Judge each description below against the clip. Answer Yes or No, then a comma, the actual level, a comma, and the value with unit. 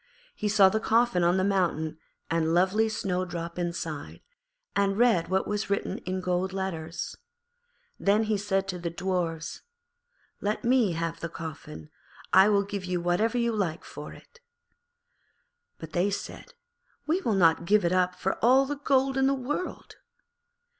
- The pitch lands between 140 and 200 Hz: Yes, high, 190 Hz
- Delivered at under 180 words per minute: Yes, average, 160 wpm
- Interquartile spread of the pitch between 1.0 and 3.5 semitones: No, average, 3.9 semitones